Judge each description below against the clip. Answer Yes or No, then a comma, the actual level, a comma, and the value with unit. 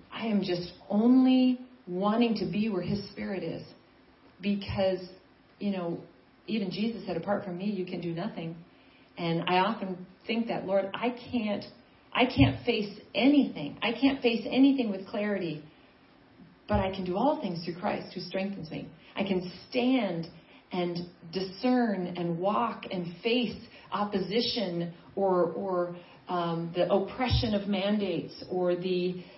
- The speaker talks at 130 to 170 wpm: Yes, average, 145 wpm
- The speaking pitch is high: Yes, high, 195 Hz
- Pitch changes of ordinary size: Yes, average, 3.4 semitones